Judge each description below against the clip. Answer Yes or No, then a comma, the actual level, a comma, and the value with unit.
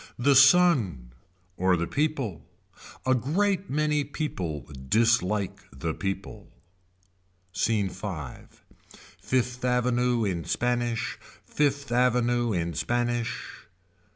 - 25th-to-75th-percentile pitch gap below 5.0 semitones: No, wide, 5.6 semitones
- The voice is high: No, low, 120 Hz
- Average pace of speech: No, slow, 95 wpm